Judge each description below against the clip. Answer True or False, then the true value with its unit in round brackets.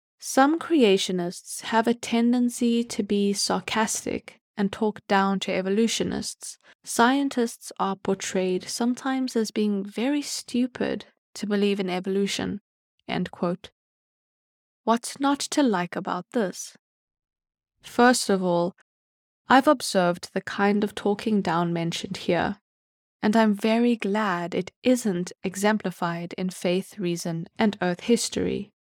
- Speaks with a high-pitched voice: True (205 Hz)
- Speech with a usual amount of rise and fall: True (3.9 semitones)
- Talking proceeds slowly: True (120 wpm)